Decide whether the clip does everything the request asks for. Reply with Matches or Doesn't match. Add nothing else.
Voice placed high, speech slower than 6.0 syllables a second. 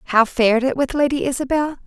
Matches